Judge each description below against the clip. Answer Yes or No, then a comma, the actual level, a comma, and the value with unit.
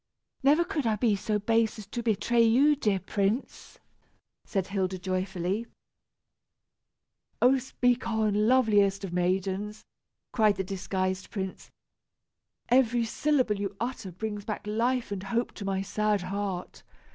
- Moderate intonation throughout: Yes, average, 3.4 semitones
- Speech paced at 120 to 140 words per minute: Yes, slow, 135 wpm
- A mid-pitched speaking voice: No, high, 210 Hz